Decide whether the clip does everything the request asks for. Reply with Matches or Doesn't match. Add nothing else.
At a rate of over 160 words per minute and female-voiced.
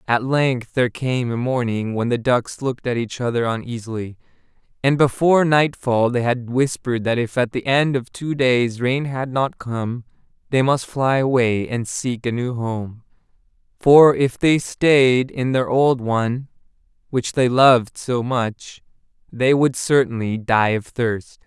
Doesn't match